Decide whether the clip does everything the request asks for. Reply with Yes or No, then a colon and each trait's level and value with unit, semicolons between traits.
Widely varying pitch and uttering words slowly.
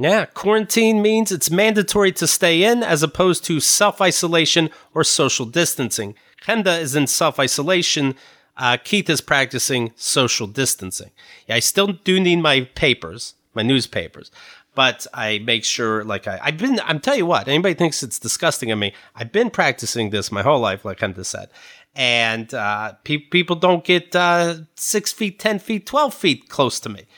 No: wide, 7.4 semitones; average, 175 wpm